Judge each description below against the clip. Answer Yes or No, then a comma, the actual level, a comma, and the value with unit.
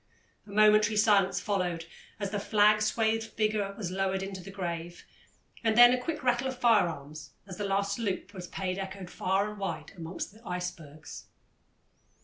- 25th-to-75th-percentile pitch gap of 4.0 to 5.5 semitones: No, average, 2.8 semitones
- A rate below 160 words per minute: No, average, 165 wpm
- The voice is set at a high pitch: Yes, high, 200 Hz